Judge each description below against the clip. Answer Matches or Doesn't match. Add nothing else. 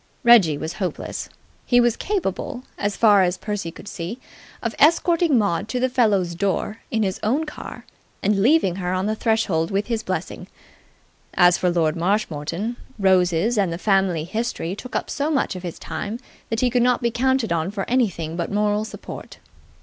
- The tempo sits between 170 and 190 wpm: Matches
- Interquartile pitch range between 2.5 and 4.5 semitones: Doesn't match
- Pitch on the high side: Matches